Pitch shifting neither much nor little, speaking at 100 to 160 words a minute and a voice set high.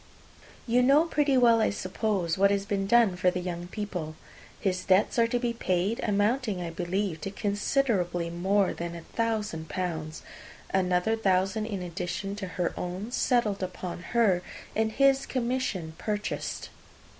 Yes: average, 4.2 semitones; average, 155 wpm; high, 195 Hz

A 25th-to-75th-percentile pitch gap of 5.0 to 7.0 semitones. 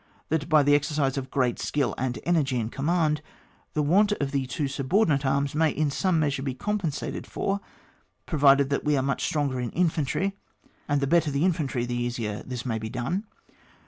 No: average, 3.2 semitones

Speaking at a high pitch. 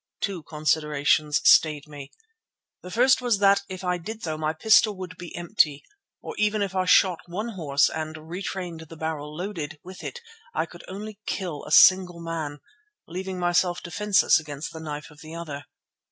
No: medium, 170 Hz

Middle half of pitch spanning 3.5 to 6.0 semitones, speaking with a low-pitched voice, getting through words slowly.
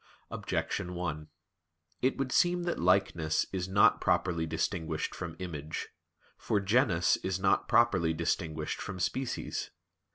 Yes: average, 3.9 semitones; very low, 90 Hz; slow, 125 wpm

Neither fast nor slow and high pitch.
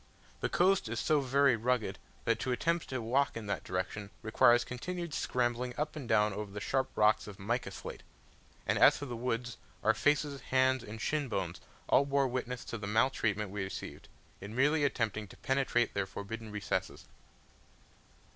No: average, 175 wpm; low, 120 Hz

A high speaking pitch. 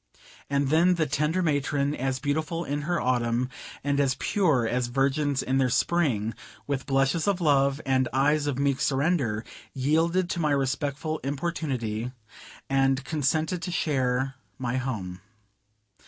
No: medium, 140 Hz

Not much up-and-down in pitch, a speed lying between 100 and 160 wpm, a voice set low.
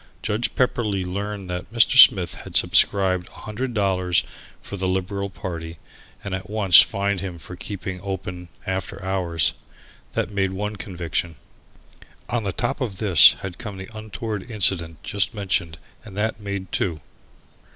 Yes: narrow, 2.3 semitones; average, 150 wpm; very low, 95 Hz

